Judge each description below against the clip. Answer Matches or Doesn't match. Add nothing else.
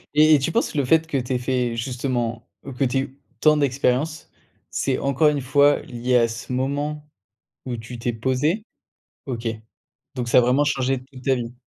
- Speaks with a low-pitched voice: Matches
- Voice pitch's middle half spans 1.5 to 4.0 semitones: Matches